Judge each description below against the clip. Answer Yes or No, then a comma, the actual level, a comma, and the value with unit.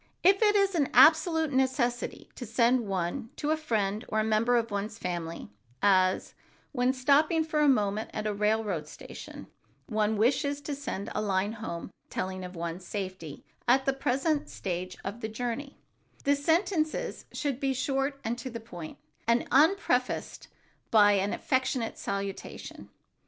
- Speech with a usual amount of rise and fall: No, wide, 5.7 semitones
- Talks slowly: No, average, 155 wpm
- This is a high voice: Yes, high, 235 Hz